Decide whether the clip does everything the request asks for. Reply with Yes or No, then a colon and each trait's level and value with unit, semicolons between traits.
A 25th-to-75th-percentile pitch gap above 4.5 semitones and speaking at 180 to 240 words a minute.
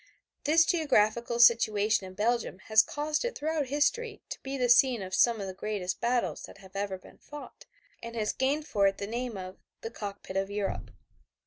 Yes: average, 5.3 semitones; average, 195 wpm